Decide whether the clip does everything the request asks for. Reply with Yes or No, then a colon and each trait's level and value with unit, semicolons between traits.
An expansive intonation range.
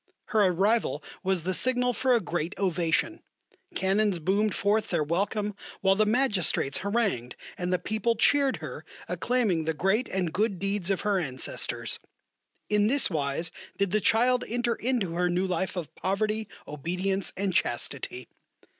No: average, 3.8 semitones